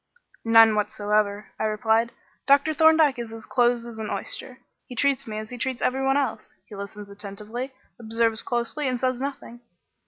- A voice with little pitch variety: No, average, 3.4 semitones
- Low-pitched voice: No, high, 235 Hz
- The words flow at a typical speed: Yes, average, 175 wpm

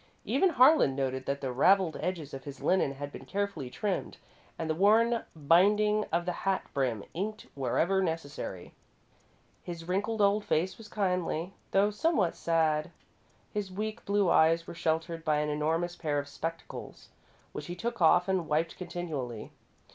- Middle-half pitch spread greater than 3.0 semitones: Yes, average, 4.8 semitones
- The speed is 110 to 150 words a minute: No, average, 160 wpm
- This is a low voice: No, medium, 170 Hz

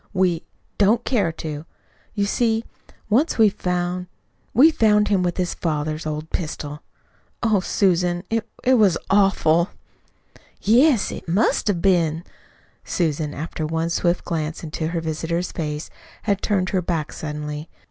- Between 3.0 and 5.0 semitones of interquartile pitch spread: Yes, average, 4.3 semitones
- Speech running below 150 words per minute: Yes, average, 140 wpm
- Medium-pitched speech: Yes, medium, 175 Hz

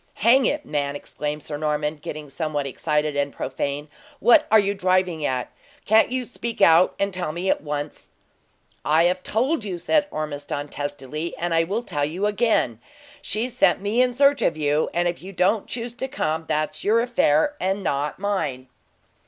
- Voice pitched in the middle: Yes, medium, 170 Hz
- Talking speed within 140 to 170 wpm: No, average, 180 wpm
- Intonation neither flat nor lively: No, wide, 6.3 semitones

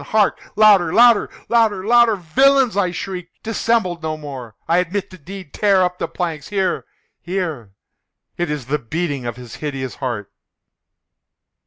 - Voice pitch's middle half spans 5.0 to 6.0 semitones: Yes, wide, 5.6 semitones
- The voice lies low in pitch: No, medium, 180 Hz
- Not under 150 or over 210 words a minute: No, slow, 135 wpm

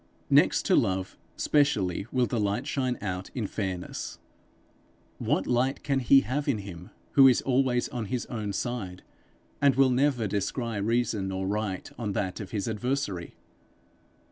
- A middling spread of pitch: Yes, average, 4.7 semitones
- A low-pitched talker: Yes, low, 115 Hz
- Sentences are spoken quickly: No, average, 155 wpm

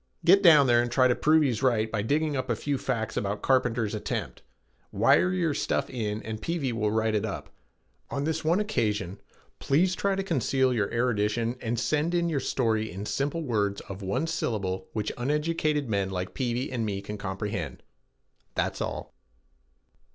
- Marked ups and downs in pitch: Yes, wide, 5.8 semitones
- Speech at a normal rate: Yes, average, 180 wpm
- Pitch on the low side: Yes, low, 120 Hz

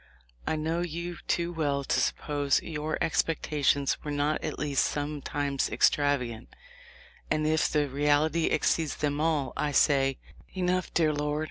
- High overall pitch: No, medium, 150 Hz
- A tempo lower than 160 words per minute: Yes, average, 140 wpm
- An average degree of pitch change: No, narrow, 1.8 semitones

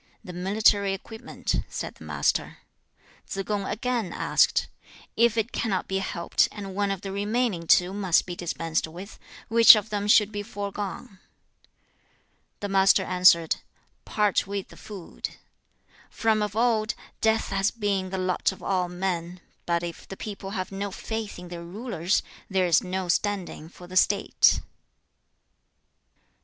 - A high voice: Yes, high, 195 Hz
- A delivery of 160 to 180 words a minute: No, average, 150 wpm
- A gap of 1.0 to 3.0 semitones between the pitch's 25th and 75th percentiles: Yes, narrow, 2.4 semitones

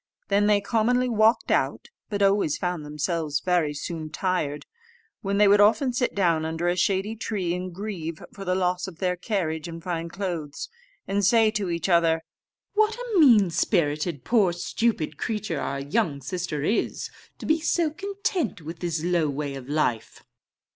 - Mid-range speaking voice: Yes, medium, 180 Hz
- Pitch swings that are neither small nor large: Yes, average, 4.7 semitones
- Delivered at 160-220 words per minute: Yes, average, 170 wpm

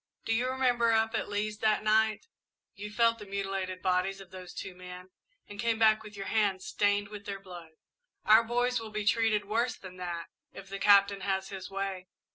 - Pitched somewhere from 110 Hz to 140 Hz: No, high, 205 Hz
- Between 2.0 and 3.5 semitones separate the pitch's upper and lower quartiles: Yes, narrow, 2.4 semitones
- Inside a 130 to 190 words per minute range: No, average, 200 wpm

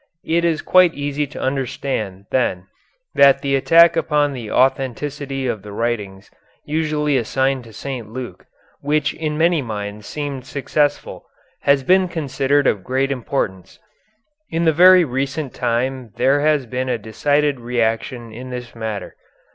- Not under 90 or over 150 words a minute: Yes, average, 145 wpm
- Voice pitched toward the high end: No, low, 135 Hz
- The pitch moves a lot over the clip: No, average, 3.8 semitones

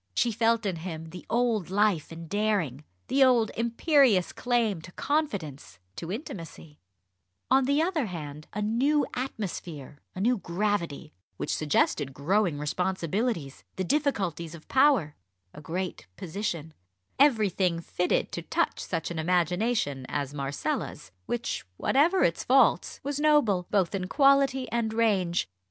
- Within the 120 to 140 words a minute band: Yes, slow, 135 wpm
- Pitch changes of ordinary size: No, wide, 6.7 semitones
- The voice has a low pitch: No, high, 195 Hz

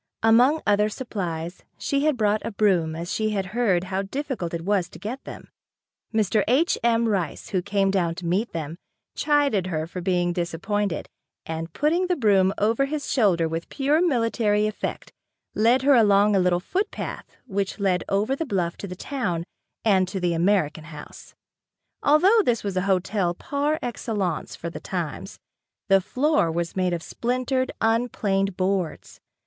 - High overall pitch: Yes, high, 200 Hz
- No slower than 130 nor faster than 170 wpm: Yes, average, 165 wpm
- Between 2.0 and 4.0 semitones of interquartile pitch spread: No, average, 5.1 semitones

